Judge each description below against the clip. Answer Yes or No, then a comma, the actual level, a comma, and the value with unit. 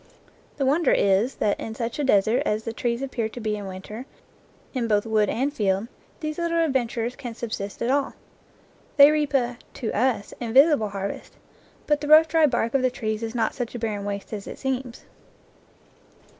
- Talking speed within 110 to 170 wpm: No, average, 200 wpm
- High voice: Yes, high, 235 Hz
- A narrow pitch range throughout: No, average, 4.0 semitones